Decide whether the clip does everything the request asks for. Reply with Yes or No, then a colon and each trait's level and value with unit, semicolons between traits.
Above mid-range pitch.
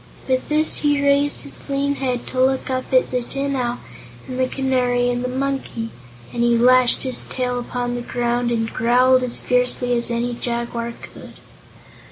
Yes: very high, 250 Hz